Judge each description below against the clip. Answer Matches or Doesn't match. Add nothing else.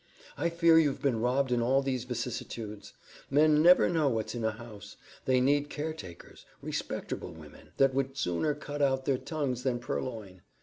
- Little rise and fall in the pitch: Doesn't match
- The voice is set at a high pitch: Doesn't match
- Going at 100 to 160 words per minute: Doesn't match